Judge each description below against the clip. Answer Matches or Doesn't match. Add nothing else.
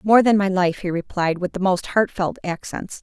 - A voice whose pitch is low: Doesn't match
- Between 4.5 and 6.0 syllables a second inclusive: Matches